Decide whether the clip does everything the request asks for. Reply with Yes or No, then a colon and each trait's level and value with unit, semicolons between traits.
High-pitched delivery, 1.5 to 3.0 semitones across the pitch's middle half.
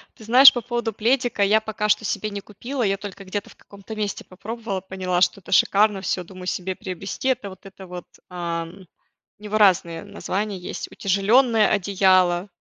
Yes: high, 200 Hz; narrow, 2.6 semitones